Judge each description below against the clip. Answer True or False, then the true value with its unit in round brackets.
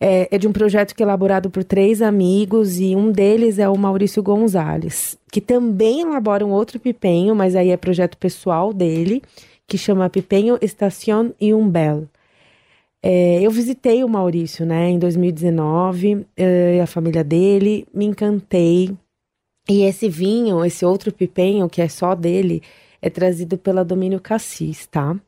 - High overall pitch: True (195 Hz)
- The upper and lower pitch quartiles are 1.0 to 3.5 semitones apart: True (2.8 semitones)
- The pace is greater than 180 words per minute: False (155 wpm)